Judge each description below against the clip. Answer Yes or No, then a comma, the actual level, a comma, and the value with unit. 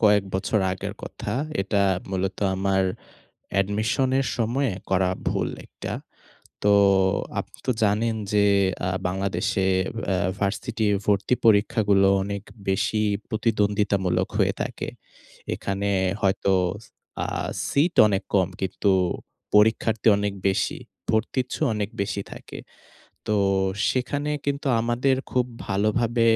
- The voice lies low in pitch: Yes, low, 105 Hz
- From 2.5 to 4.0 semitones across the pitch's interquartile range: Yes, average, 2.8 semitones